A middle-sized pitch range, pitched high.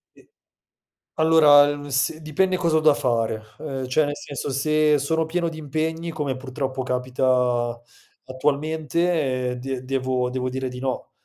No: average, 3.3 semitones; medium, 140 Hz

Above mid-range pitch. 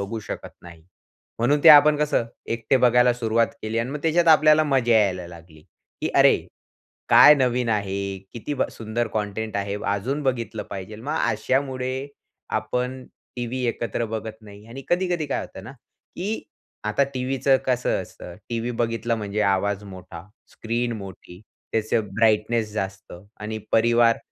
No: low, 115 Hz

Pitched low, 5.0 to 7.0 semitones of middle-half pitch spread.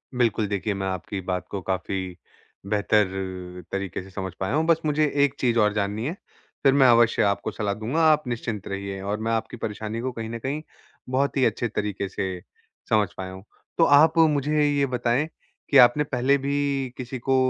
Yes: low, 115 Hz; wide, 5.6 semitones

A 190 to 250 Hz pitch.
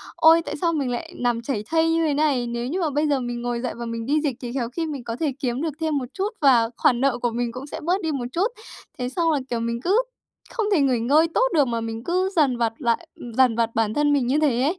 No: very high, 265 Hz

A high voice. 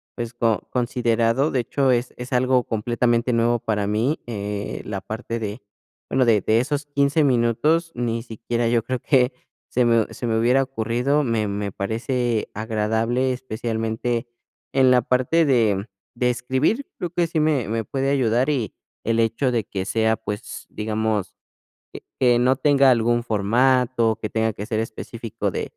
No: low, 120 Hz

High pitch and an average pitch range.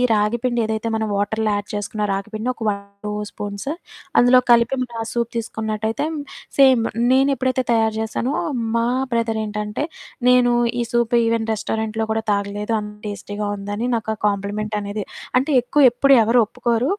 No: high, 220 Hz; narrow, 2.3 semitones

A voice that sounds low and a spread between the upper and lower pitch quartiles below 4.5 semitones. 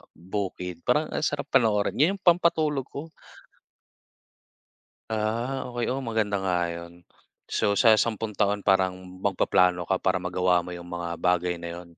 No: low, 100 Hz; wide, 5.5 semitones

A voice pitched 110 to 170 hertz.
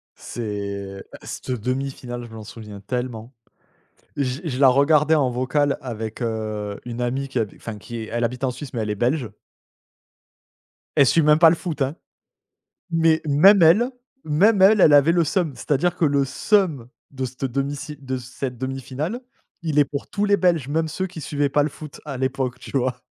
Yes: low, 135 Hz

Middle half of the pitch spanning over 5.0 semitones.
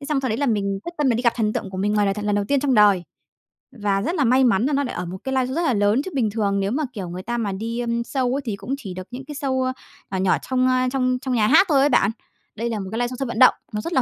No: average, 4.4 semitones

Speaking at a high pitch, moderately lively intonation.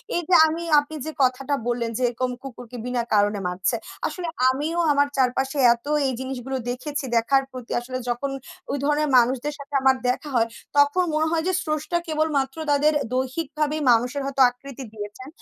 Yes: very high, 270 Hz; average, 3.2 semitones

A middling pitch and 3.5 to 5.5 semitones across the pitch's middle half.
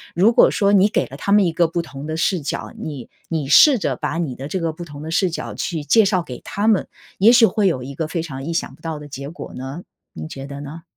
Yes: medium, 165 Hz; average, 4.8 semitones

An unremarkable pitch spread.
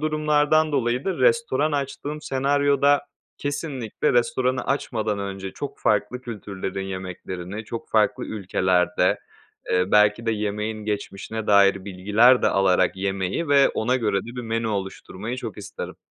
No: wide, 5.8 semitones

